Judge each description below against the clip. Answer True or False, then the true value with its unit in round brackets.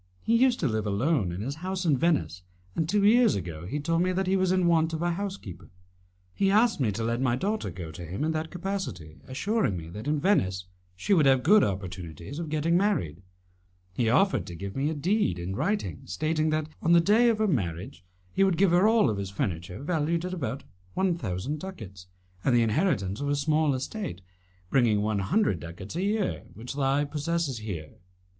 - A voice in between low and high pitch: True (150 Hz)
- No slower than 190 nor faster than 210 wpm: True (205 wpm)